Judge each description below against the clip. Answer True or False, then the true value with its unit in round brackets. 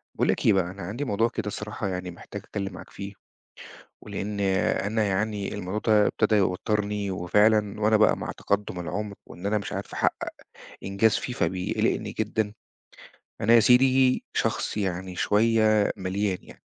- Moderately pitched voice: False (105 Hz)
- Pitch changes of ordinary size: False (2.0 semitones)